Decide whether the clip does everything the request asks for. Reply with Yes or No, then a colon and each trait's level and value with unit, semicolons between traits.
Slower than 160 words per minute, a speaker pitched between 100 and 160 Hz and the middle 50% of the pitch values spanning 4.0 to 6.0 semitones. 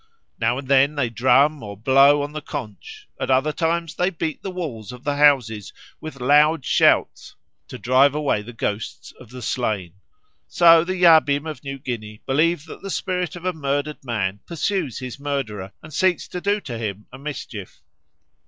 No: average, 180 wpm; medium, 140 Hz; average, 4.8 semitones